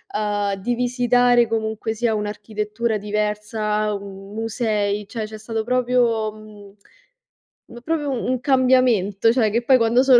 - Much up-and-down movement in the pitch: No, narrow, 2.6 semitones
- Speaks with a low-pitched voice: No, high, 220 Hz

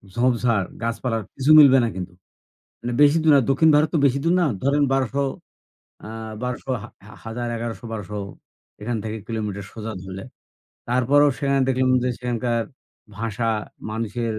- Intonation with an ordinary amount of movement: Yes, average, 3.2 semitones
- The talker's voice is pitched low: Yes, low, 120 Hz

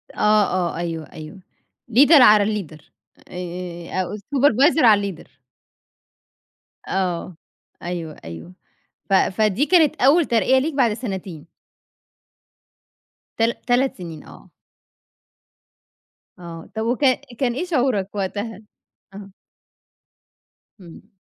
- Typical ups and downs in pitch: No, wide, 5.8 semitones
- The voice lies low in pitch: No, high, 205 Hz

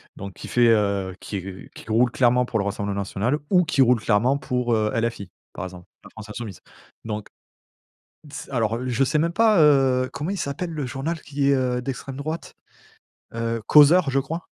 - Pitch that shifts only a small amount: No, average, 4.6 semitones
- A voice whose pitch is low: Yes, low, 125 Hz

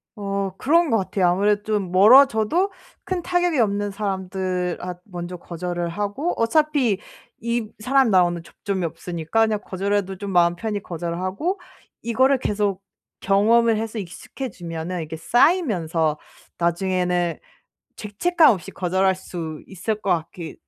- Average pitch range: Yes, average, 4.1 semitones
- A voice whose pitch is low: No, high, 195 Hz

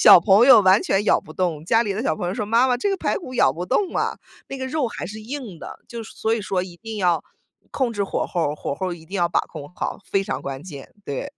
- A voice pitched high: Yes, high, 200 Hz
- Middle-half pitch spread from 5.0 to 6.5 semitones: Yes, average, 5.3 semitones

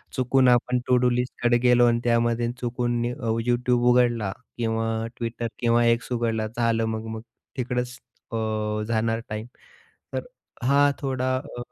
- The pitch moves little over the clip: Yes, narrow, 1.3 semitones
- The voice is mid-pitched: No, low, 120 Hz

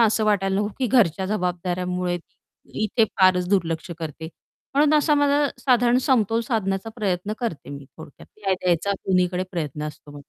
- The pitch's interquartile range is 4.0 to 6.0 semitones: Yes, average, 4.3 semitones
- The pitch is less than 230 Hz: Yes, high, 190 Hz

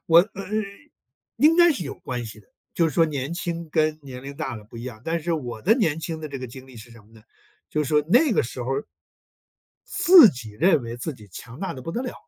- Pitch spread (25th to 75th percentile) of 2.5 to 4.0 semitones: No, wide, 5.6 semitones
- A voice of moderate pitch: Yes, medium, 150 Hz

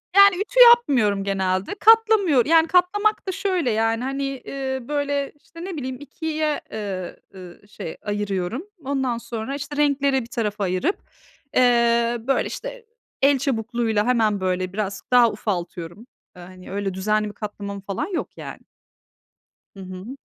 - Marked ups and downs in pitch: Yes, wide, 6.3 semitones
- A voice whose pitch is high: Yes, high, 240 Hz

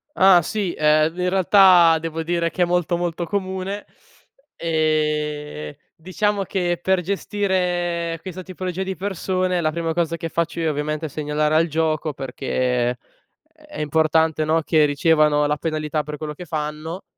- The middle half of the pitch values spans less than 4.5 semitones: Yes, average, 2.9 semitones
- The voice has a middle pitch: Yes, medium, 165 Hz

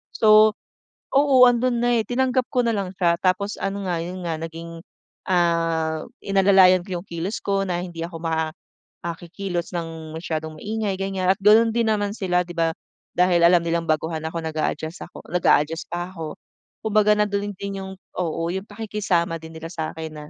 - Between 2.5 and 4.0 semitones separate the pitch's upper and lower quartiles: Yes, average, 3.5 semitones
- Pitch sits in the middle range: Yes, medium, 180 Hz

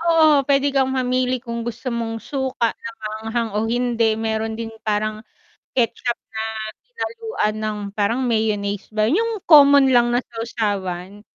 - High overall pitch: Yes, high, 235 Hz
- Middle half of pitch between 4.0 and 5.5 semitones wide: No, average, 3.5 semitones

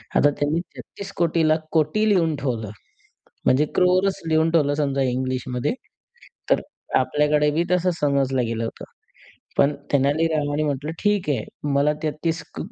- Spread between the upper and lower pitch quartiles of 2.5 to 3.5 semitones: Yes, average, 2.8 semitones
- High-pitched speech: No, medium, 150 Hz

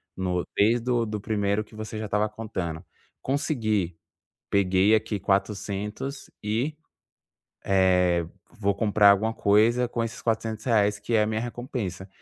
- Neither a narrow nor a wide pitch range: No, narrow, 2.3 semitones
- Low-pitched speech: Yes, low, 105 Hz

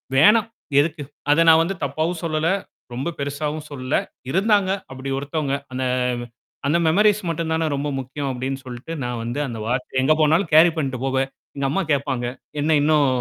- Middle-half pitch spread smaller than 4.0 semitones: Yes, average, 3.4 semitones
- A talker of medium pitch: Yes, medium, 145 Hz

